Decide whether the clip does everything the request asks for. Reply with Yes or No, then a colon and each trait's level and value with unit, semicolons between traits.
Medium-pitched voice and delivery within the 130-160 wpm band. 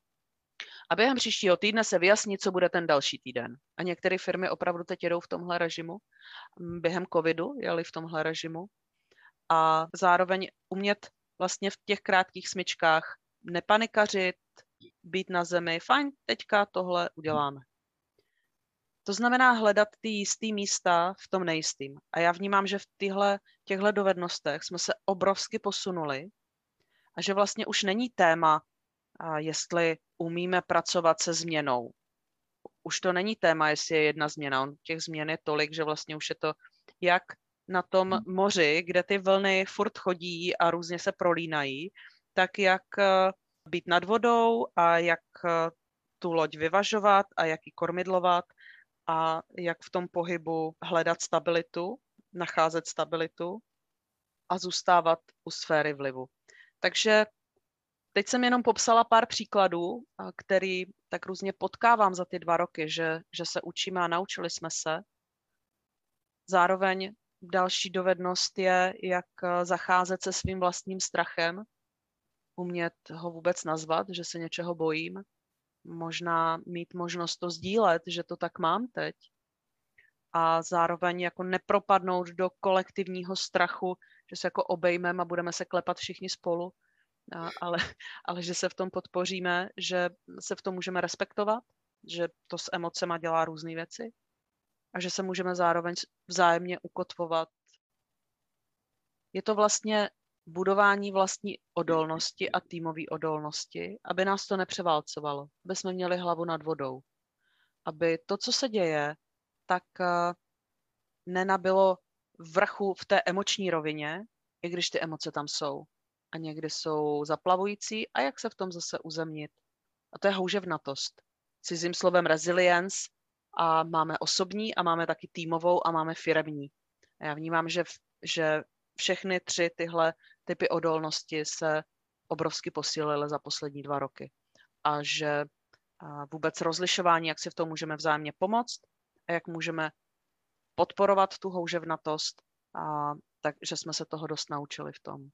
Yes: medium, 175 Hz; average, 140 wpm